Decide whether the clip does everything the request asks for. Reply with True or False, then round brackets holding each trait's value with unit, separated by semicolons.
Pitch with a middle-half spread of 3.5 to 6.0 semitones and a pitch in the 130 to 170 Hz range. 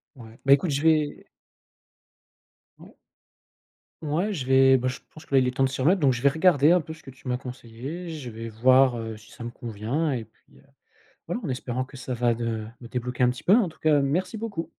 True (4.4 semitones; 135 Hz)